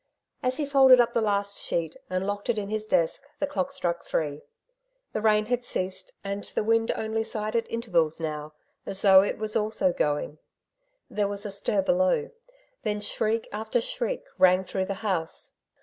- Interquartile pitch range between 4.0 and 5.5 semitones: No, average, 3.4 semitones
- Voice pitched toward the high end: Yes, high, 210 Hz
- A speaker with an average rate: Yes, average, 180 wpm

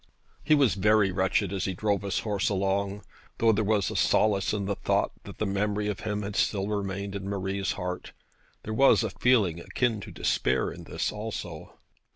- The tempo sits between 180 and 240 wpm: Yes, average, 195 wpm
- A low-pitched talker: Yes, low, 100 Hz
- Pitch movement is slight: Yes, narrow, 1.7 semitones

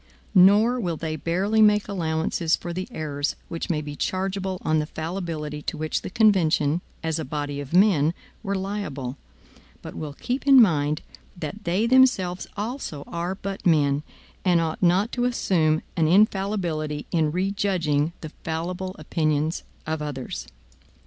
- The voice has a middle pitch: Yes, medium, 170 Hz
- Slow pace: No, average, 150 wpm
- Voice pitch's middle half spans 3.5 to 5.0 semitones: Yes, average, 4.1 semitones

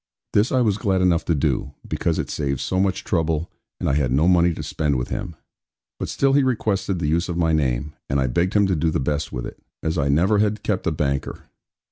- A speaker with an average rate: No, fast, 240 wpm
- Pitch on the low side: Yes, very low, 85 Hz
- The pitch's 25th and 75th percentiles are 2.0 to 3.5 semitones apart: No, average, 5.1 semitones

